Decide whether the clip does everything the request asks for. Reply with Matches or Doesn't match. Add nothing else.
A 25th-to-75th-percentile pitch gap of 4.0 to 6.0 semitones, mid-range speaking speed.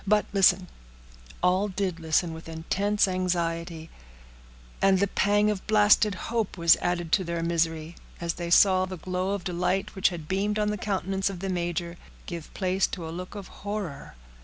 Doesn't match